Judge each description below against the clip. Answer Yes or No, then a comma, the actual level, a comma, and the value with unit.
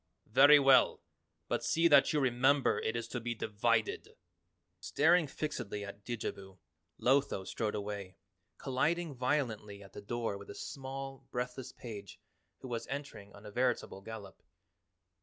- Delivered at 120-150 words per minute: Yes, average, 140 wpm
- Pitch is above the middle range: No, low, 120 Hz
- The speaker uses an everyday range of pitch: Yes, average, 4.8 semitones